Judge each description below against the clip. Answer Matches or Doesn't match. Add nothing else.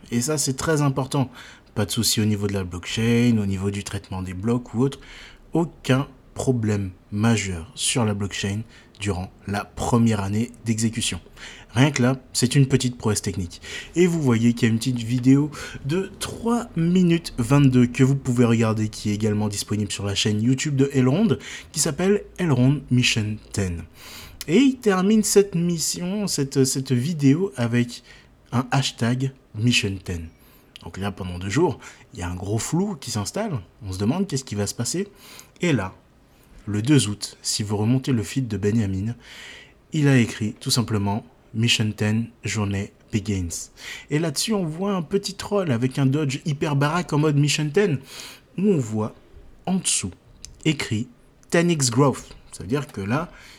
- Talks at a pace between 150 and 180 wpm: Matches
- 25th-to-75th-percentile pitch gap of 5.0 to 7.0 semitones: Matches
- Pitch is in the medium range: Doesn't match